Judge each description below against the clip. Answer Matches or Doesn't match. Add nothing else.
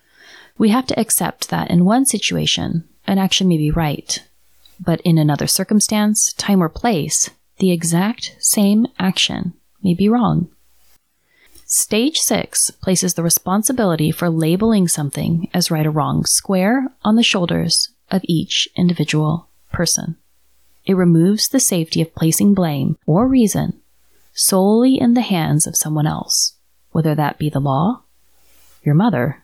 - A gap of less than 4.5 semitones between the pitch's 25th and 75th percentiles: Doesn't match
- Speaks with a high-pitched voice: Doesn't match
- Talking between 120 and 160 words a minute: Matches